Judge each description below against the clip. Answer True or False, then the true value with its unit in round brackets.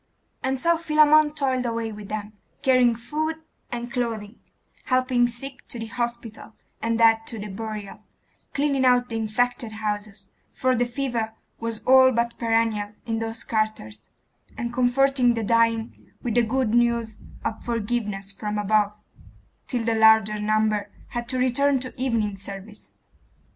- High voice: True (230 Hz)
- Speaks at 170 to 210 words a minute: False (150 wpm)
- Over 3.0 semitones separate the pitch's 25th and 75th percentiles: False (2.6 semitones)